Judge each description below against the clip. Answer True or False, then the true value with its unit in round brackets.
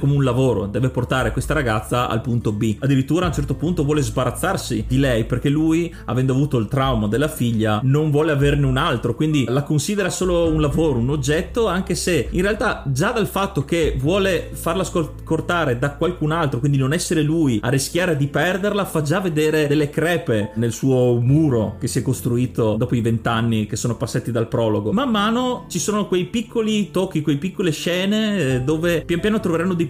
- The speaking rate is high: True (195 wpm)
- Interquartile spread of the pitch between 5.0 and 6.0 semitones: True (5.4 semitones)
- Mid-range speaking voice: True (150 Hz)